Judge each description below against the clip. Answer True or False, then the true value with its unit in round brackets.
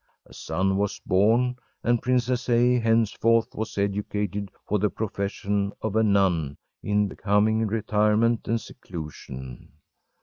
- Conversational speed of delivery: False (125 wpm)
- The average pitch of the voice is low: True (105 Hz)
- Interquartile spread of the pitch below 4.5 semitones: True (2.4 semitones)